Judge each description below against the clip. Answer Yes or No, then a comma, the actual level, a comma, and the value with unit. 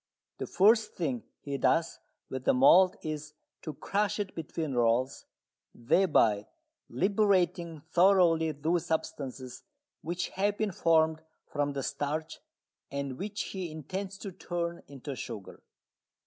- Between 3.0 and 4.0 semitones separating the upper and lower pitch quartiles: No, average, 5.1 semitones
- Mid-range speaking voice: Yes, medium, 160 Hz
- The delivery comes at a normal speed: No, slow, 125 wpm